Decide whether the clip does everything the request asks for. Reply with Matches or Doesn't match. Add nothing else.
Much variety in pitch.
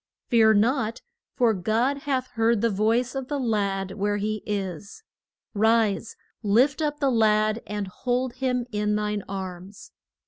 Doesn't match